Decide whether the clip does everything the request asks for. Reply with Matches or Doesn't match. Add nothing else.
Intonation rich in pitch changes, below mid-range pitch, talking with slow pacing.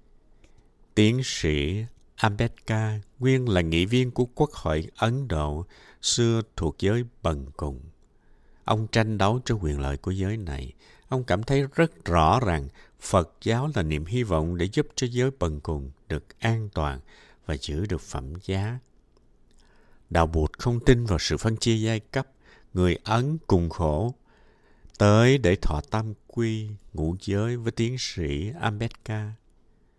Matches